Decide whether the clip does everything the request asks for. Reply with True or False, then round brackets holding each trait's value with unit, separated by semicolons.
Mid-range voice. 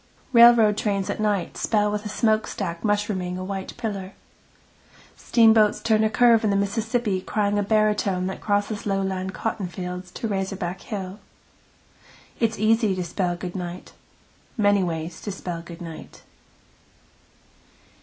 False (200 Hz)